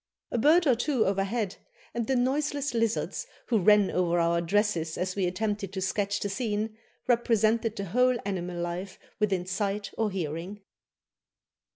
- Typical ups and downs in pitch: Yes, average, 3.8 semitones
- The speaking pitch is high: Yes, high, 205 Hz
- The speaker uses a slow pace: No, average, 155 wpm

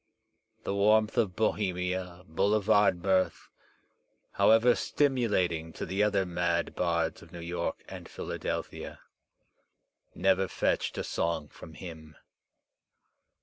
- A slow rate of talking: Yes, slow, 105 wpm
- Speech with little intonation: No, average, 3.4 semitones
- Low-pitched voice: Yes, very low, 95 Hz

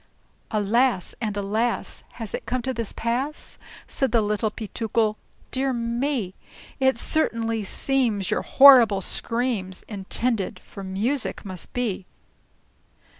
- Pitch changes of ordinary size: Yes, average, 3.6 semitones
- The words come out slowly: Yes, slow, 120 wpm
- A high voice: Yes, high, 230 Hz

